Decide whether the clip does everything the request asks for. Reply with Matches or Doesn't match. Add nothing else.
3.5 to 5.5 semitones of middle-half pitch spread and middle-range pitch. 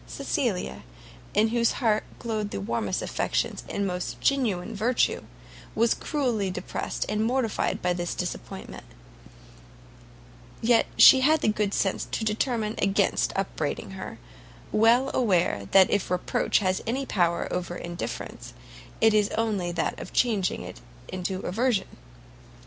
Doesn't match